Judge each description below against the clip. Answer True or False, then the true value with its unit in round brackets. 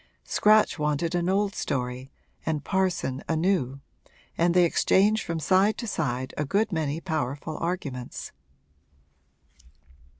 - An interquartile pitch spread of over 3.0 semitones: True (5.3 semitones)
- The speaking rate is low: True (125 wpm)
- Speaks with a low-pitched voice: False (165 Hz)